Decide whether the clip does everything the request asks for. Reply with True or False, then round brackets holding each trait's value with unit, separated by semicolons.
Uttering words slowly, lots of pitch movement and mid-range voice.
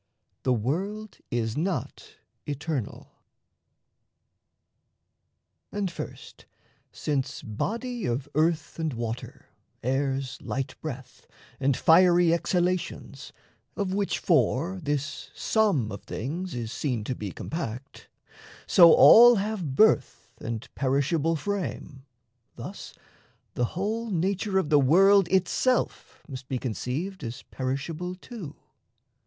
True (105 wpm; 6.4 semitones; 155 Hz)